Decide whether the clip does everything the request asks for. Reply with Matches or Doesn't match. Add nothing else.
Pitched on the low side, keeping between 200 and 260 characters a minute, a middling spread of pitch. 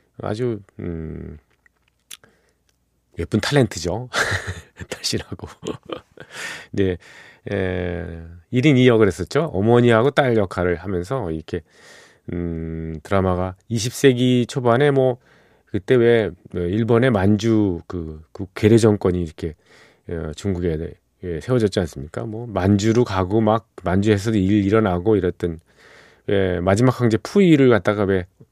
Matches